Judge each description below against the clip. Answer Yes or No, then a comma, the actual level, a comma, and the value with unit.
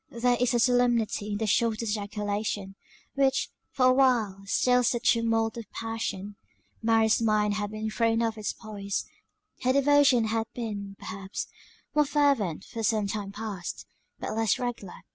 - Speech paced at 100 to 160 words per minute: Yes, average, 155 wpm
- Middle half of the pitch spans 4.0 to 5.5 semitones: No, average, 2.8 semitones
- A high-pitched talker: Yes, high, 225 Hz